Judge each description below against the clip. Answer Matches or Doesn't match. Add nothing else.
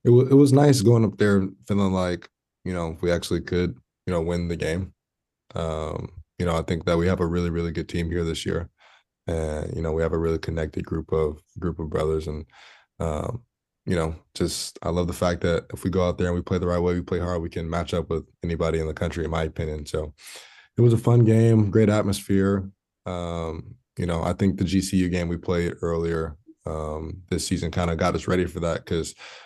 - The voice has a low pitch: Matches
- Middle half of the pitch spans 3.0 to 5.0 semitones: Doesn't match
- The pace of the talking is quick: Matches